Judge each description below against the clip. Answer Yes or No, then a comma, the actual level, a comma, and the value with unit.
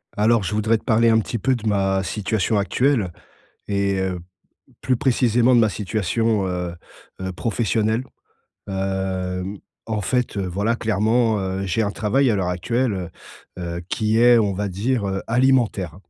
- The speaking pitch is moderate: No, low, 105 Hz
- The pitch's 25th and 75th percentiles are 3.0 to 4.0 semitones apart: Yes, average, 3.3 semitones